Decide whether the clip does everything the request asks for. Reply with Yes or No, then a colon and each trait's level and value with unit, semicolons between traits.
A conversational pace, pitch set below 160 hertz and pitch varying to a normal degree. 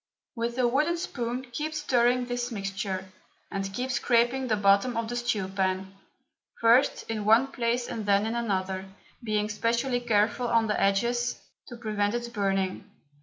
No: average, 160 wpm; high, 230 Hz; average, 3.2 semitones